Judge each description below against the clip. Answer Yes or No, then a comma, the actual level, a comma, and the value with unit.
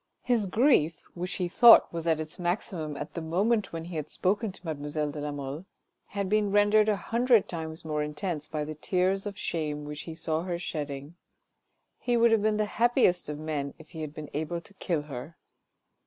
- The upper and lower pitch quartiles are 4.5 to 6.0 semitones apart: Yes, average, 5.0 semitones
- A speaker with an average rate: No, fast, 210 wpm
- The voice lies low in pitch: No, medium, 170 Hz